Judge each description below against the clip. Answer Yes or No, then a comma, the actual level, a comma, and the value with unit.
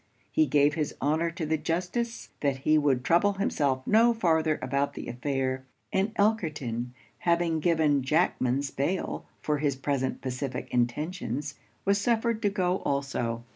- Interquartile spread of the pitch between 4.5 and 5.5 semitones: Yes, average, 5.1 semitones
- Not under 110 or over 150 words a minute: Yes, average, 145 wpm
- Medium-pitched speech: Yes, medium, 150 Hz